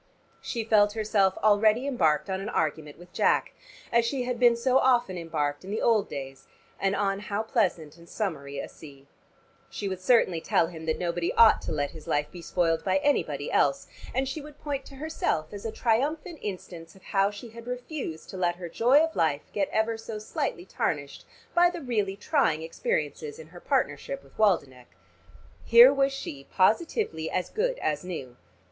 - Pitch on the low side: No, high, 200 Hz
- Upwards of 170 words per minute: Yes, average, 190 wpm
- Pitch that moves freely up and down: Yes, wide, 7.2 semitones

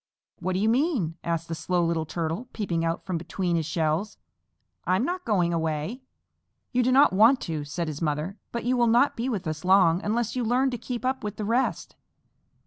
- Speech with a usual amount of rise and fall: No, wide, 6.4 semitones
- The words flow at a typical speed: No, fast, 210 wpm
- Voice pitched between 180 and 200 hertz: Yes, high, 190 Hz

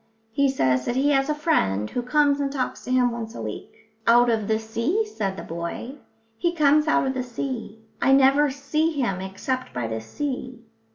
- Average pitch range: Yes, average, 4.4 semitones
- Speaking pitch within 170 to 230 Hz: No, very high, 255 Hz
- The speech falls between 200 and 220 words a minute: Yes, fast, 205 wpm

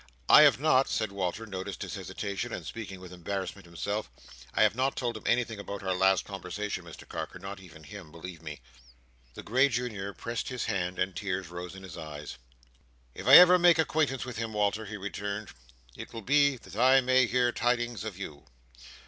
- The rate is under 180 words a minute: No, average, 195 wpm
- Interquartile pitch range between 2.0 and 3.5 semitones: No, average, 4.7 semitones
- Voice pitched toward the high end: No, low, 100 Hz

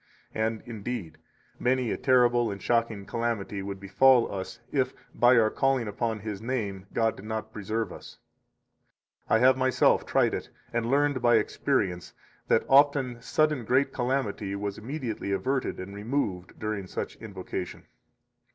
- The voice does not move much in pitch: No, average, 4.1 semitones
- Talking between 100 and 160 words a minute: Yes, average, 150 wpm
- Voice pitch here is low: Yes, low, 115 Hz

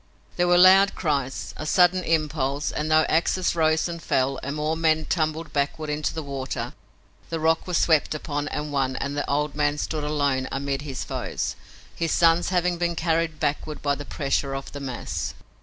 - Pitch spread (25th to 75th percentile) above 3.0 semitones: No, narrow, 2.6 semitones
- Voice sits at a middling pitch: Yes, medium, 155 Hz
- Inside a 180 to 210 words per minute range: Yes, average, 190 wpm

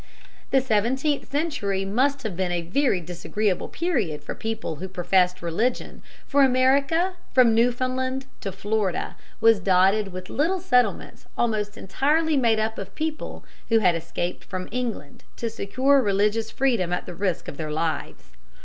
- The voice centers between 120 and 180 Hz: No, high, 220 Hz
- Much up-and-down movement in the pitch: Yes, wide, 6.0 semitones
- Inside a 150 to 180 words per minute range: Yes, average, 155 wpm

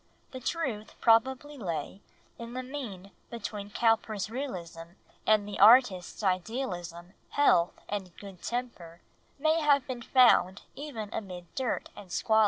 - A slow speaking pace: Yes, slow, 130 wpm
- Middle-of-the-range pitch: No, high, 220 Hz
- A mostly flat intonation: No, wide, 5.6 semitones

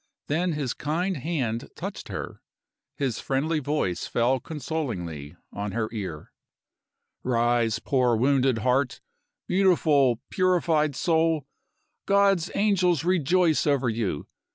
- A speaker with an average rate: No, slow, 105 wpm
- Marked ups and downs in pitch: Yes, wide, 5.8 semitones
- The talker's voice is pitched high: No, medium, 140 Hz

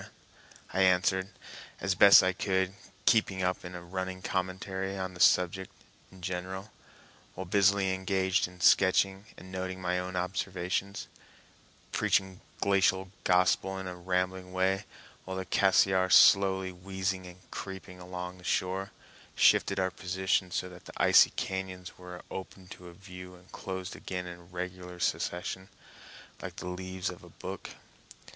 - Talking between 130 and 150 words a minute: Yes, average, 140 wpm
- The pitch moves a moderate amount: No, narrow, 0.8 semitones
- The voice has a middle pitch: No, very low, 95 Hz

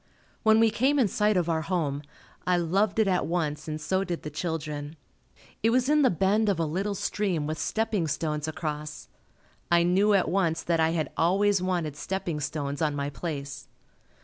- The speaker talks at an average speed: Yes, average, 190 wpm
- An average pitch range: Yes, average, 4.6 semitones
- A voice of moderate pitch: Yes, medium, 170 Hz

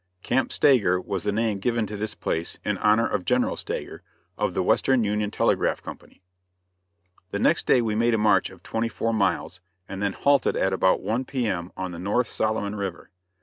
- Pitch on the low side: Yes, low, 105 Hz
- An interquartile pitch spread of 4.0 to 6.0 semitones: No, average, 3.1 semitones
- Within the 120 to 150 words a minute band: No, average, 195 wpm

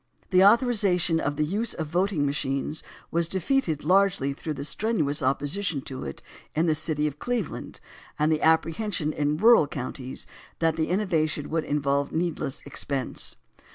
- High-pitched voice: No, medium, 155 Hz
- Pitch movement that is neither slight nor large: Yes, average, 4.3 semitones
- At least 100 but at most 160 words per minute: Yes, average, 155 wpm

